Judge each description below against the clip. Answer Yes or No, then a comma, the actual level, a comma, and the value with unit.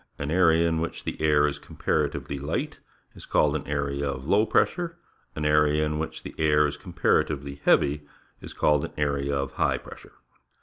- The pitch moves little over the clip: Yes, narrow, 1.7 semitones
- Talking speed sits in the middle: Yes, average, 180 wpm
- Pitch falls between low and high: No, very low, 75 Hz